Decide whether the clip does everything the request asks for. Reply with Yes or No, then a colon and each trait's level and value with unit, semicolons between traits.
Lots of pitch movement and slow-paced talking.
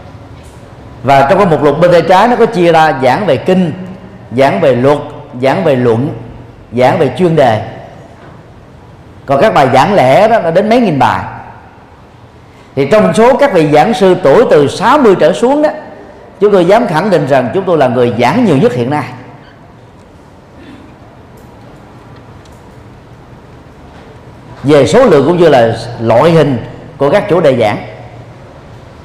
Yes: wide, 7.1 semitones; slow, 160 wpm